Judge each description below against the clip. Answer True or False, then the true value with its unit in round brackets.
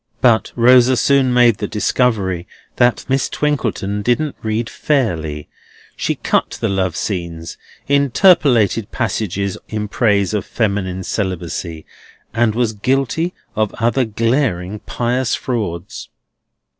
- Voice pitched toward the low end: True (110 Hz)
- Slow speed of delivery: True (115 wpm)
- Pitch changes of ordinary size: True (4.4 semitones)